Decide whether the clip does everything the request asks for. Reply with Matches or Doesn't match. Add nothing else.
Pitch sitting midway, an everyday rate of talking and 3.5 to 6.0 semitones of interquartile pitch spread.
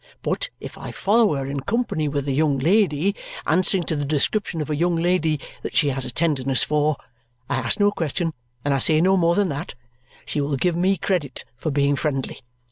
Doesn't match